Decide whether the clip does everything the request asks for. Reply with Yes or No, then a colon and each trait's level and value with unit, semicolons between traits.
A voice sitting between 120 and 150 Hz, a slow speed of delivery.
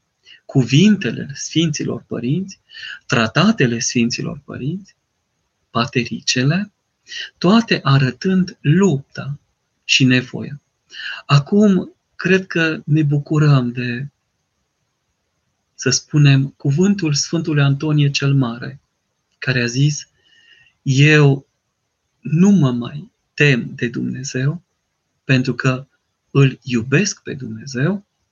Yes: medium, 140 Hz; slow, 85 wpm